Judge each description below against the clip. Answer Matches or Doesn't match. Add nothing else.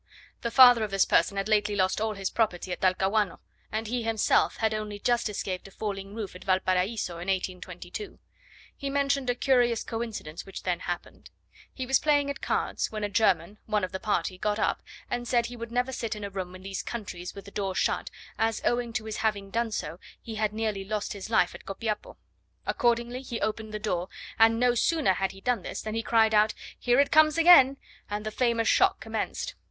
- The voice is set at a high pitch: Matches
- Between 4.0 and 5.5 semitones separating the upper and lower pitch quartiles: Doesn't match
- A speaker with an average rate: Doesn't match